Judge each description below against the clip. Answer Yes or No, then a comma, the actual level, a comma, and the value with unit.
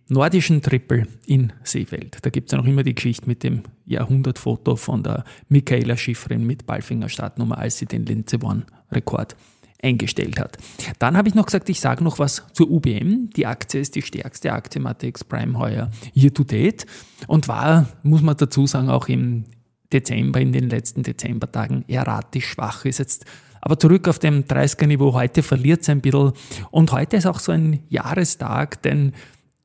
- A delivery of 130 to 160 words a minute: No, average, 180 wpm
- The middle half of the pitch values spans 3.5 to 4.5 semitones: Yes, average, 4.2 semitones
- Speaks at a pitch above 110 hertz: Yes, low, 135 Hz